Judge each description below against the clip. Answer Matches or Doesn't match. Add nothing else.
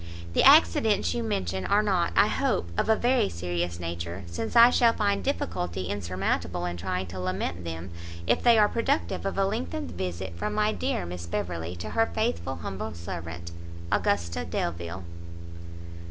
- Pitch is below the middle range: Matches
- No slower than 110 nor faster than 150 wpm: Doesn't match